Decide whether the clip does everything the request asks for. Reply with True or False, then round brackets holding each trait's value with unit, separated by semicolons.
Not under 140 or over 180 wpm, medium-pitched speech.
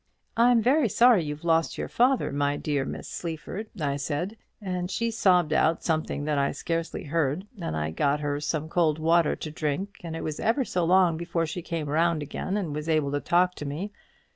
False (205 wpm; 165 Hz)